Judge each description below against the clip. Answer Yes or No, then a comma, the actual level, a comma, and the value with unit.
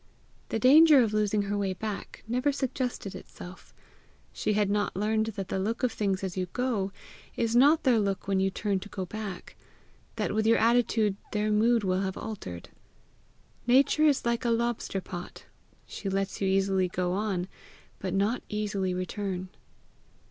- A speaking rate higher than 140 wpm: Yes, average, 170 wpm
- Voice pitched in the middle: No, high, 205 Hz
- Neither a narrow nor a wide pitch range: Yes, average, 3.2 semitones